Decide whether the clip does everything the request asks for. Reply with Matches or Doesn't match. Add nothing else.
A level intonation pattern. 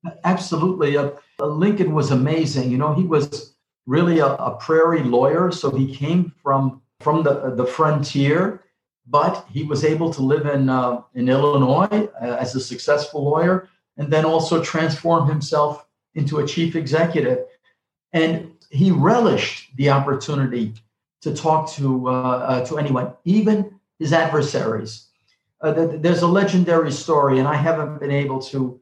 Doesn't match